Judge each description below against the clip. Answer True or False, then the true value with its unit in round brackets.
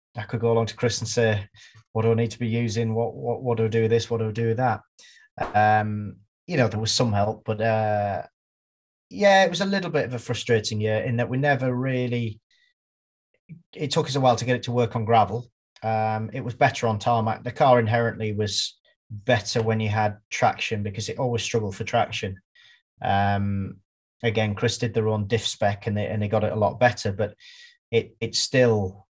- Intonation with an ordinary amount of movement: False (2.2 semitones)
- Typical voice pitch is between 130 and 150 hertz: False (115 Hz)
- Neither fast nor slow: False (220 wpm)